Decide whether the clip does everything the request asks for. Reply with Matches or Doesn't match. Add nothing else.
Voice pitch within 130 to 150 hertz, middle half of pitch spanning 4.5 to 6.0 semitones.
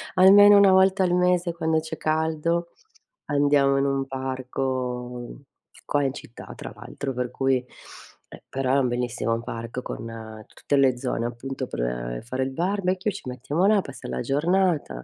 Matches